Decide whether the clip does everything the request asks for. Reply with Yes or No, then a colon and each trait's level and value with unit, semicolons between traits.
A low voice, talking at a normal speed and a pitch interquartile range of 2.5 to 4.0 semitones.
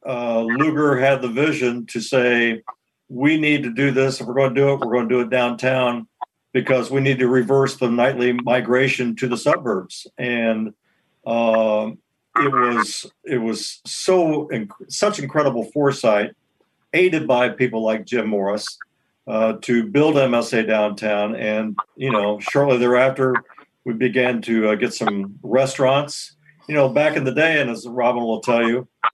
Yes: low, 125 Hz; average, 165 wpm; average, 2.9 semitones